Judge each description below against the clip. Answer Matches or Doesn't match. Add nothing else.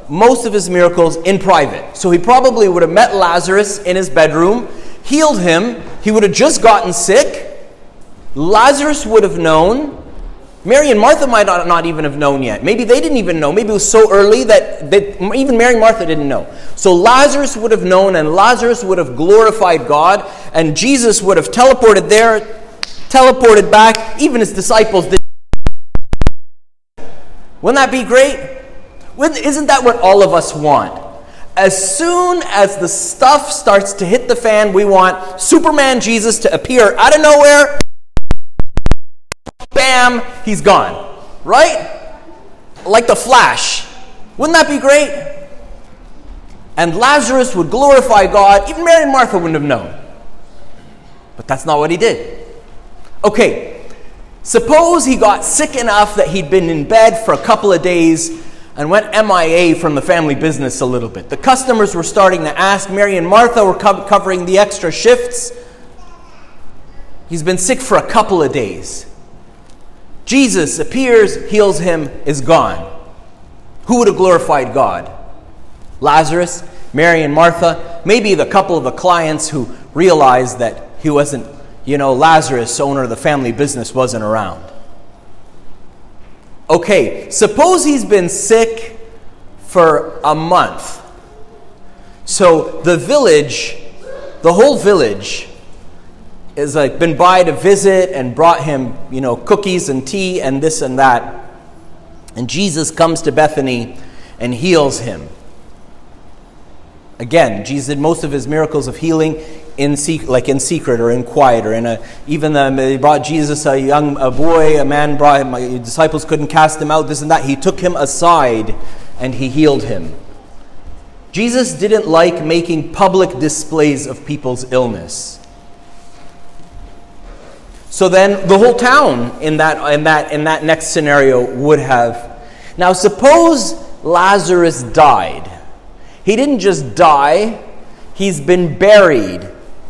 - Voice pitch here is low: Doesn't match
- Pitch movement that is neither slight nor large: Doesn't match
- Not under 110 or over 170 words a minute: Matches